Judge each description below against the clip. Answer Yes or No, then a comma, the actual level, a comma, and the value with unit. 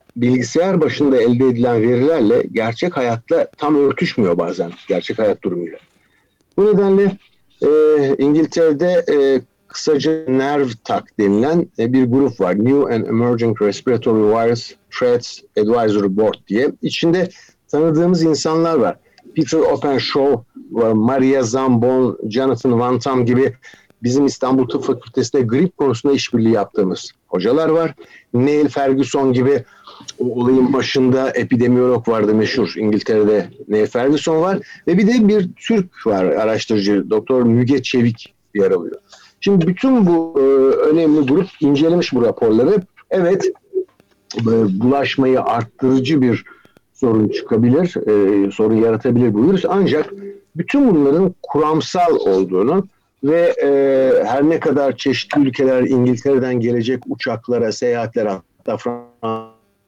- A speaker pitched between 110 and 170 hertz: Yes, low, 135 Hz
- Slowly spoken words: No, average, 115 wpm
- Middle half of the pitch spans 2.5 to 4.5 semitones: No, average, 5.2 semitones